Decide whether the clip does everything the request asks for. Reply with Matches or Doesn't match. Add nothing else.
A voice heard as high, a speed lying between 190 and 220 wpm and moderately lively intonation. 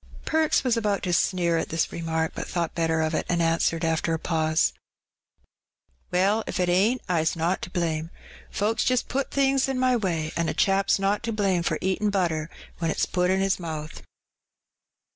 Doesn't match